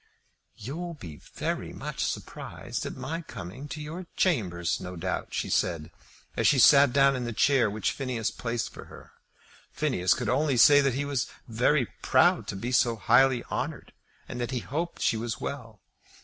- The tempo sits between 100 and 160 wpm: No, average, 175 wpm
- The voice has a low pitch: Yes, low, 125 Hz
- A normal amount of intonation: Yes, average, 4.4 semitones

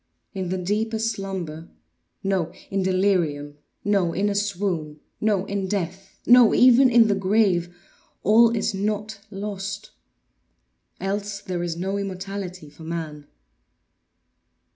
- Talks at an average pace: No, slow, 105 wpm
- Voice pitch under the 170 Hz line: No, high, 195 Hz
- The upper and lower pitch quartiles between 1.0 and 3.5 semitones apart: Yes, average, 2.8 semitones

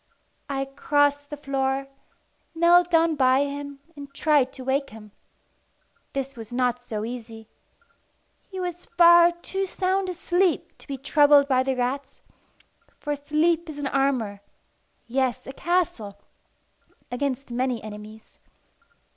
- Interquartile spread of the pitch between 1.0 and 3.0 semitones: No, average, 3.9 semitones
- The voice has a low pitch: No, very high, 275 Hz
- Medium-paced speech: No, slow, 130 wpm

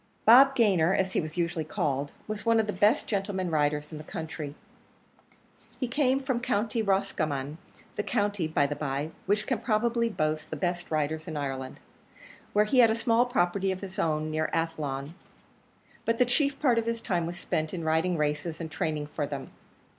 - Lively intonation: Yes, wide, 6.2 semitones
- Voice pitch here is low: No, medium, 175 Hz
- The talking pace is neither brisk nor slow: Yes, average, 190 wpm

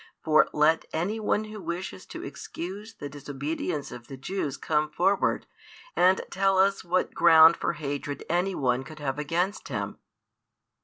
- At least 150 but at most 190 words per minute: Yes, average, 155 wpm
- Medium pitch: Yes, medium, 165 Hz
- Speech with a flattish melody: No, average, 4.7 semitones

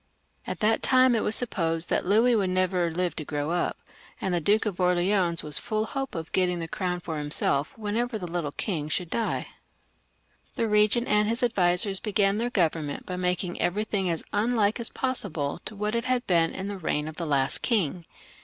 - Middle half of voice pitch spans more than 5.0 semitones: No, average, 4.3 semitones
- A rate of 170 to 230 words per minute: Yes, average, 200 wpm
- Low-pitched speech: No, medium, 185 Hz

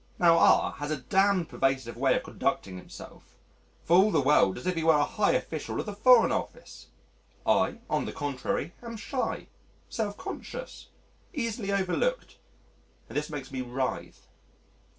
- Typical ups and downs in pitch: No, wide, 7.2 semitones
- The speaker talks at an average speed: Yes, average, 160 wpm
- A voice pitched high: No, medium, 165 Hz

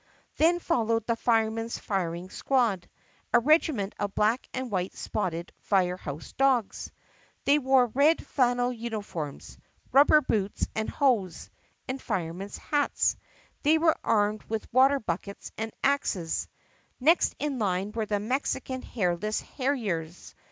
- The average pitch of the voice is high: Yes, high, 225 Hz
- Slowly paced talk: Yes, slow, 130 wpm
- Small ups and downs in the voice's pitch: No, average, 5.3 semitones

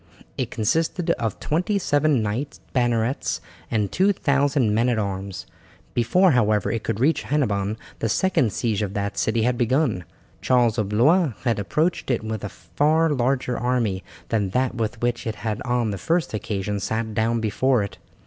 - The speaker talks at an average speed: Yes, average, 170 wpm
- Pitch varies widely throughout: No, average, 4.6 semitones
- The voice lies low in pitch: Yes, low, 115 Hz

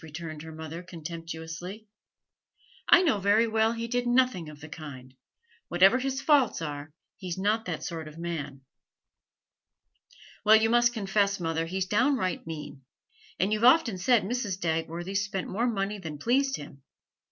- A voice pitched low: No, high, 190 Hz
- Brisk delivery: No, average, 155 wpm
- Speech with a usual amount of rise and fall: No, wide, 5.7 semitones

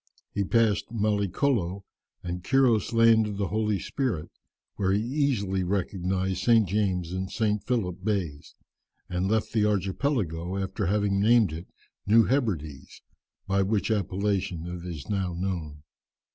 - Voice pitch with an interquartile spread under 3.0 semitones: No, average, 3.3 semitones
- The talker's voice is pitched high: No, low, 100 Hz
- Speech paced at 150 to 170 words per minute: No, slow, 135 wpm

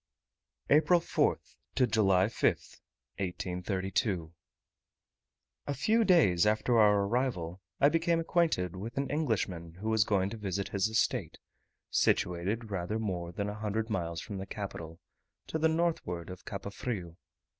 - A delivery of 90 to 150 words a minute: Yes, average, 140 wpm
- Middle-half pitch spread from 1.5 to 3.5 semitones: No, average, 5.2 semitones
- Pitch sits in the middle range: No, low, 105 Hz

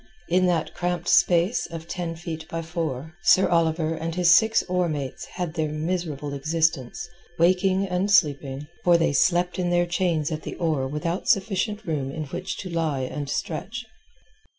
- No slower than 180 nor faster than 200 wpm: No, average, 165 wpm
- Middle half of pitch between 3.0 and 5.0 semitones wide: No, narrow, 2.5 semitones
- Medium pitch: Yes, medium, 165 Hz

